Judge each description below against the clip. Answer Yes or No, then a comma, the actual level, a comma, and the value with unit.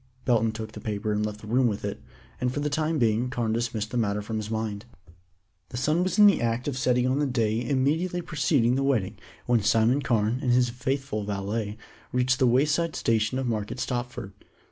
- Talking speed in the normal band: No, fast, 210 wpm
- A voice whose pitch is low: Yes, low, 120 Hz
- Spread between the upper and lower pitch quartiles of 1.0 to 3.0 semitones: No, average, 3.5 semitones